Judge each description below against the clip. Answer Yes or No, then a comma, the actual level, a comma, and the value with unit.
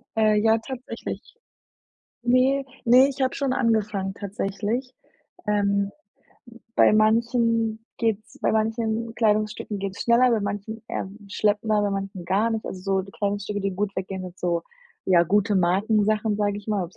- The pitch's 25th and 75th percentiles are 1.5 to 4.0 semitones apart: Yes, narrow, 2.4 semitones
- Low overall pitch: No, high, 210 Hz